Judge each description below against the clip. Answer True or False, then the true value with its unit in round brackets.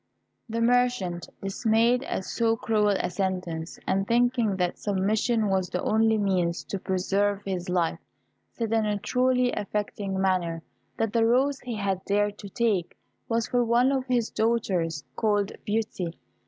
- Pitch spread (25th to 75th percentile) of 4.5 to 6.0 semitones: False (3.4 semitones)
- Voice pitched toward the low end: False (205 Hz)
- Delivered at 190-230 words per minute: False (155 wpm)